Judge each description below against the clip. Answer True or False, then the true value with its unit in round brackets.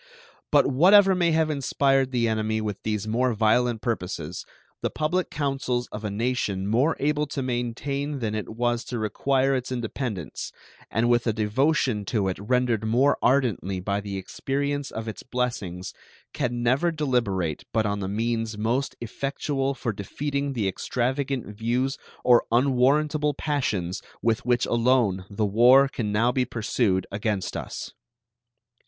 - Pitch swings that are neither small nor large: True (4.1 semitones)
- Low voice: True (120 Hz)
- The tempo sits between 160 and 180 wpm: False (150 wpm)